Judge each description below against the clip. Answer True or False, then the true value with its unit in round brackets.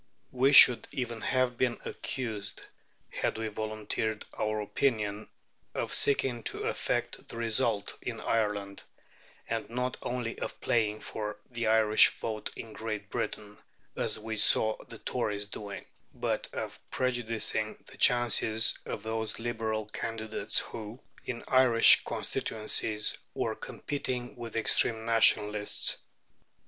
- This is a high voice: False (110 Hz)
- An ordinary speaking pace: False (125 wpm)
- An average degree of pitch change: False (1.9 semitones)